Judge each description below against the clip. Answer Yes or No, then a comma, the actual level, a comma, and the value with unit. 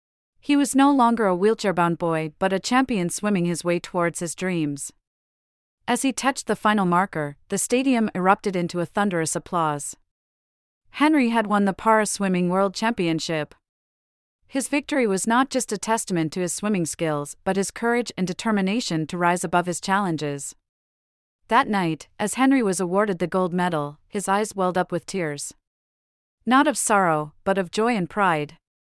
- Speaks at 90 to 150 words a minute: No, average, 170 wpm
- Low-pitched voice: No, medium, 185 Hz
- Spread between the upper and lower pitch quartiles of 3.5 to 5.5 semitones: Yes, average, 4.8 semitones